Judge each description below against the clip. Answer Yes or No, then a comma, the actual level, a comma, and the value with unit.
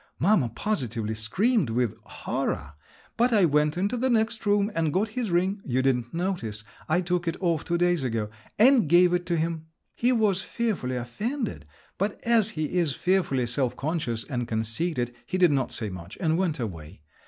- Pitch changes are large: Yes, wide, 8.3 semitones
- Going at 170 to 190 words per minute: Yes, average, 175 wpm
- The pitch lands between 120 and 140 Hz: No, medium, 165 Hz